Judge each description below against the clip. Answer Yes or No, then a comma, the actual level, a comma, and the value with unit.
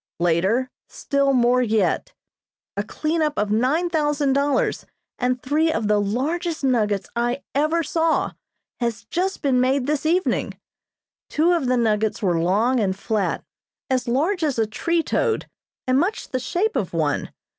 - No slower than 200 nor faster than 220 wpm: No, average, 155 wpm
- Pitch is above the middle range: Yes, very high, 260 Hz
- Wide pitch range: Yes, wide, 6.1 semitones